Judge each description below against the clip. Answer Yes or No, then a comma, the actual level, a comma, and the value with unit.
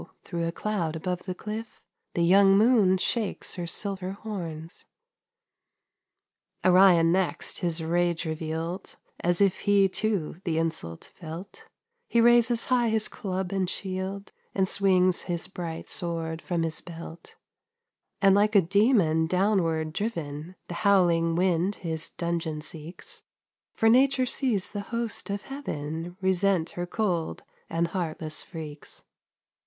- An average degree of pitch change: Yes, average, 3.4 semitones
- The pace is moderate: No, slow, 130 wpm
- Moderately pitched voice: Yes, medium, 180 Hz